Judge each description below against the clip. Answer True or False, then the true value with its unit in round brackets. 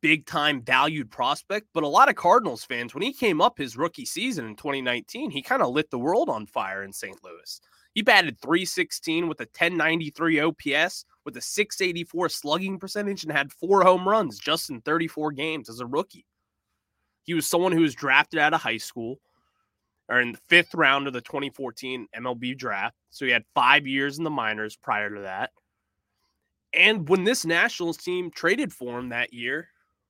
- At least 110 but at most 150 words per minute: False (190 wpm)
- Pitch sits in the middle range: True (155 Hz)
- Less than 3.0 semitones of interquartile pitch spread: False (5.3 semitones)